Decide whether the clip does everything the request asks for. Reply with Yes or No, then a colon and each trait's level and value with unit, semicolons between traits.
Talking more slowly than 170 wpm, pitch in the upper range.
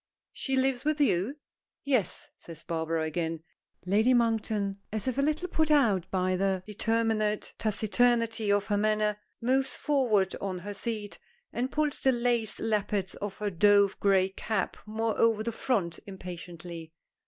Yes: average, 155 wpm; high, 210 Hz